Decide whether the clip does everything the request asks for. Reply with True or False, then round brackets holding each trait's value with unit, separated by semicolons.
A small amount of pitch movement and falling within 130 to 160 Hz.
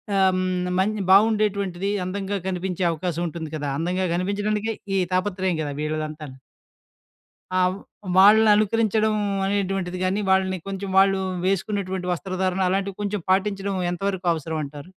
False (1.9 semitones; 190 Hz)